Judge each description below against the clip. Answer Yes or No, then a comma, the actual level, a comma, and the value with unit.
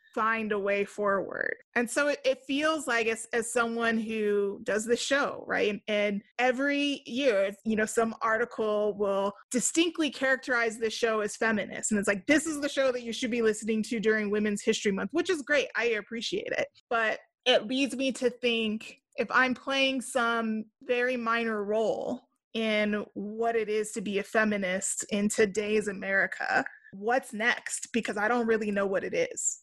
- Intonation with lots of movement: No, average, 3.3 semitones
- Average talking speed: Yes, average, 180 wpm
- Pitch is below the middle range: No, high, 230 Hz